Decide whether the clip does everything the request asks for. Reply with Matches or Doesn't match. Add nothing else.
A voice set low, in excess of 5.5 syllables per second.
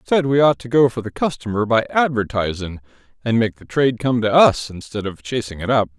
Matches